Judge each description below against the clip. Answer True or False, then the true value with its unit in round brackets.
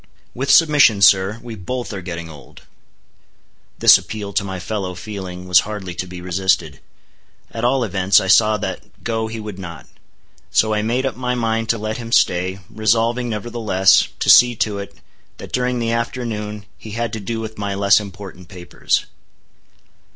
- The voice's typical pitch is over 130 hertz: False (105 Hz)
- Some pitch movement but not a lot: True (3.5 semitones)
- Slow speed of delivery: False (175 wpm)